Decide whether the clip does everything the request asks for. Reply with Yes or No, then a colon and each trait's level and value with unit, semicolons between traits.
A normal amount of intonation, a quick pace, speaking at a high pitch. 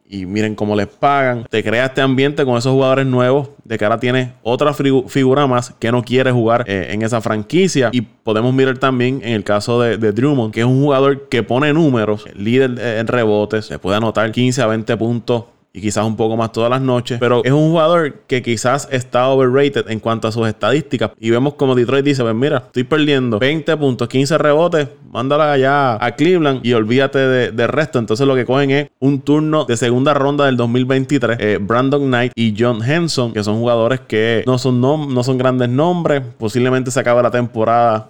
No: average, 3.1 semitones; fast, 210 wpm; low, 125 Hz